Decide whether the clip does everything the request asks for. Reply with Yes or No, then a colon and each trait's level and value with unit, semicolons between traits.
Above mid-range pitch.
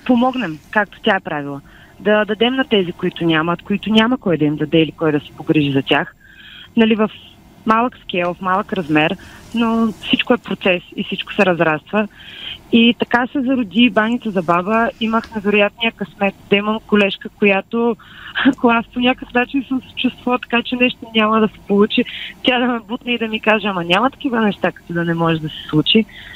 Yes: high, 215 Hz